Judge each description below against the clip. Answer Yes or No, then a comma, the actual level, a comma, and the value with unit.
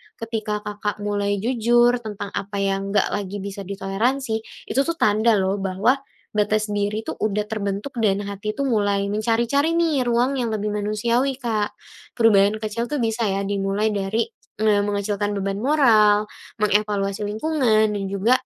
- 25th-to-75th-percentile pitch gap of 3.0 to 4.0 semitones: No, narrow, 2.5 semitones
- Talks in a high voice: Yes, high, 210 Hz